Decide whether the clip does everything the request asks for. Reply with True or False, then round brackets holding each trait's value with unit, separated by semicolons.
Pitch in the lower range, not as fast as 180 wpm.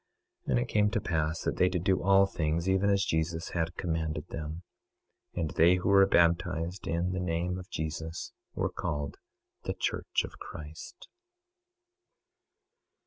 True (85 Hz; 160 wpm)